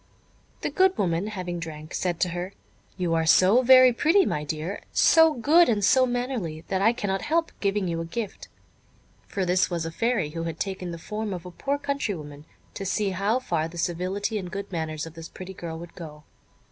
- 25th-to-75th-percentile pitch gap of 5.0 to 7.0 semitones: Yes, wide, 5.4 semitones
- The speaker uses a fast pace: Yes, fast, 210 wpm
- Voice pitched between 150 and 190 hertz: Yes, medium, 185 Hz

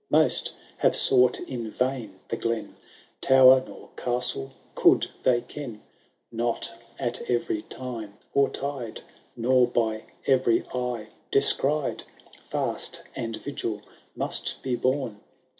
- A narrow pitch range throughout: Yes, narrow, 2.3 semitones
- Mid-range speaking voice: No, low, 125 Hz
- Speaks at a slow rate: Yes, slow, 115 wpm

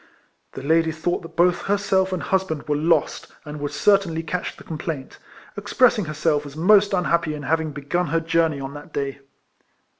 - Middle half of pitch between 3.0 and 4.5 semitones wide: Yes, average, 3.3 semitones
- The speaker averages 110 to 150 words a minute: No, average, 180 wpm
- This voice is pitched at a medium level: Yes, medium, 165 Hz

